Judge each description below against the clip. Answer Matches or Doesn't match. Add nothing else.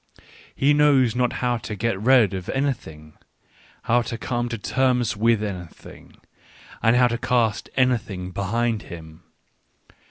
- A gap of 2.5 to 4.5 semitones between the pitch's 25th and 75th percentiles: Matches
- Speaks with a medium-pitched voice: Doesn't match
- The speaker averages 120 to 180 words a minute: Matches